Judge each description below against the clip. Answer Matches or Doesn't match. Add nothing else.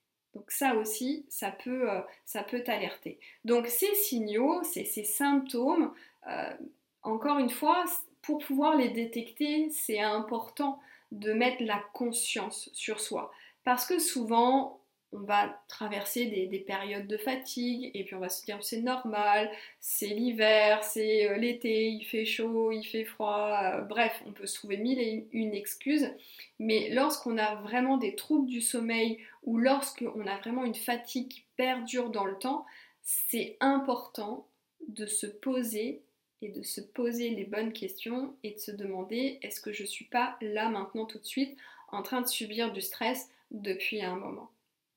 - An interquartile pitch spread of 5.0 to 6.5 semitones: Doesn't match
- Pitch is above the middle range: Matches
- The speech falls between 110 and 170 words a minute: Matches